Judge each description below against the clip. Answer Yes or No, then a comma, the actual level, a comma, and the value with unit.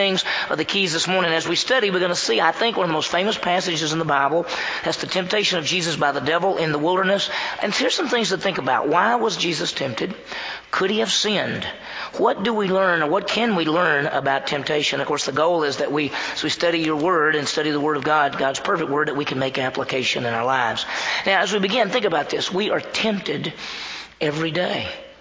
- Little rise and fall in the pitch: No, average, 4.4 semitones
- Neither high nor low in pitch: Yes, medium, 170 Hz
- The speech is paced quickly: Yes, fast, 240 wpm